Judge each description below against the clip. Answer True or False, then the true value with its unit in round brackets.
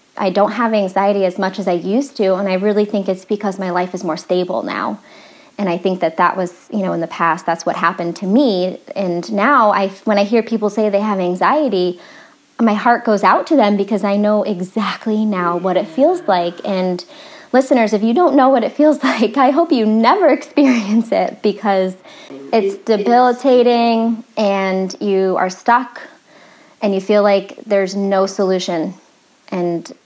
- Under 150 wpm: False (190 wpm)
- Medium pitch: False (205 Hz)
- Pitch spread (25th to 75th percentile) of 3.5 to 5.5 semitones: True (4.2 semitones)